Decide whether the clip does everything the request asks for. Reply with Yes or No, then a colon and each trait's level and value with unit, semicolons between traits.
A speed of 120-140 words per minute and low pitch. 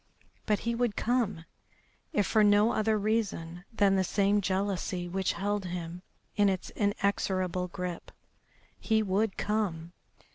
No: slow, 135 wpm; high, 200 Hz